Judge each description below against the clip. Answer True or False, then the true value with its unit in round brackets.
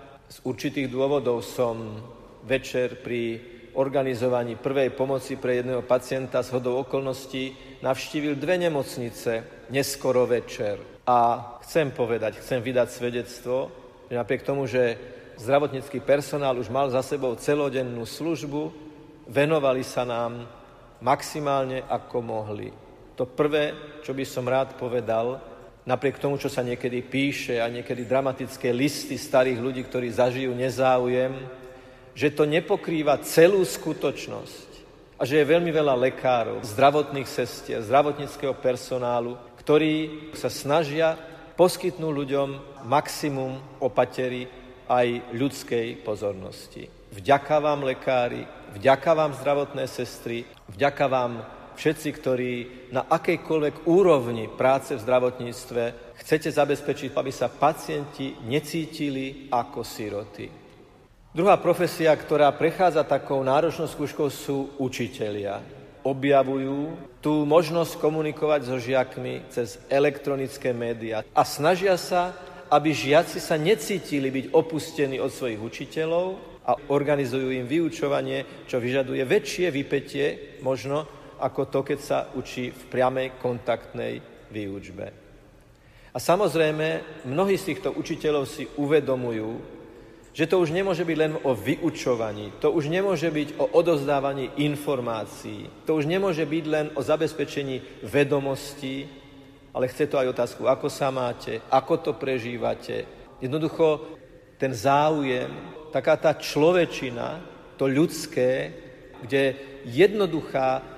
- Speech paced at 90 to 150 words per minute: True (115 wpm)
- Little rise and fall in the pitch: False (3.1 semitones)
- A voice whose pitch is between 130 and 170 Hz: True (135 Hz)